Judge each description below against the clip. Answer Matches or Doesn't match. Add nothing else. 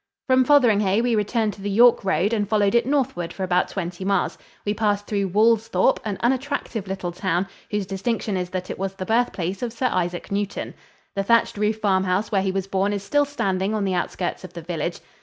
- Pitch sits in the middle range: Doesn't match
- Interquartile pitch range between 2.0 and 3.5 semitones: Matches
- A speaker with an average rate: Doesn't match